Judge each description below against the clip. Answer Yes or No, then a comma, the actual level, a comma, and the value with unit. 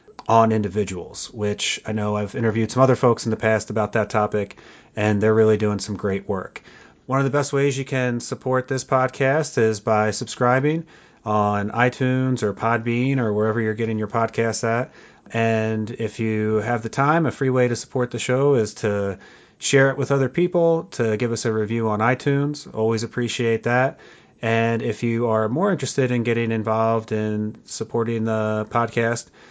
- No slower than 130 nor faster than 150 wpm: No, average, 185 wpm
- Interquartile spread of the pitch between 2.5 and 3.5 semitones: Yes, average, 2.9 semitones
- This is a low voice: Yes, low, 115 Hz